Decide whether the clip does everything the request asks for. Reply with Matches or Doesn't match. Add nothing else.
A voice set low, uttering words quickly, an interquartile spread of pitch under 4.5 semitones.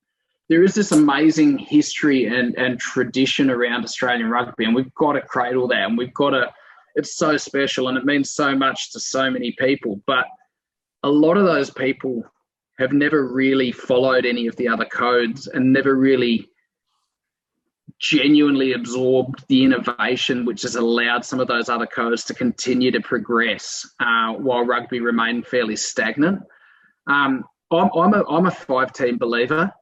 Doesn't match